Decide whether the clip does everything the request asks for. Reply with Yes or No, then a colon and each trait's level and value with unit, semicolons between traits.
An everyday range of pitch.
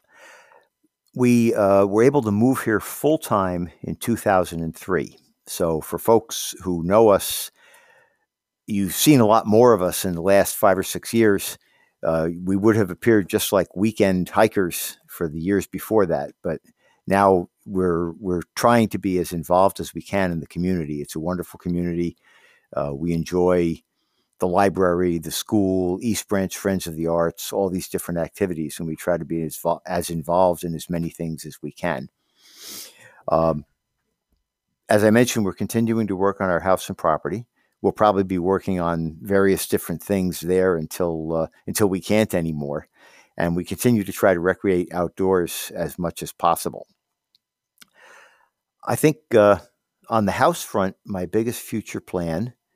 Yes: average, 3.9 semitones